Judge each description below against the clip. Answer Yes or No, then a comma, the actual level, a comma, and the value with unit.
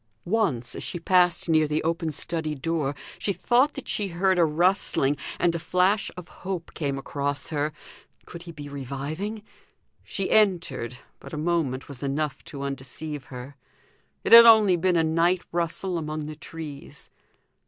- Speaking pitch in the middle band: Yes, medium, 160 Hz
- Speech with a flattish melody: No, average, 4.0 semitones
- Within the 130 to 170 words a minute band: Yes, average, 165 wpm